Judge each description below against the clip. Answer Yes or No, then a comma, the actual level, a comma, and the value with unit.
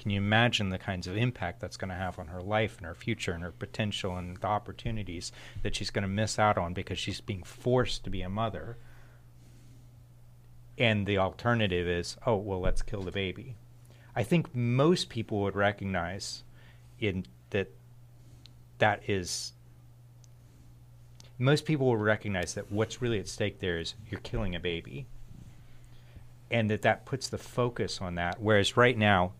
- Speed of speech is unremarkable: Yes, average, 170 wpm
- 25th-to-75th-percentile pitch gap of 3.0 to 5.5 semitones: Yes, average, 3.8 semitones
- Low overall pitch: Yes, low, 110 Hz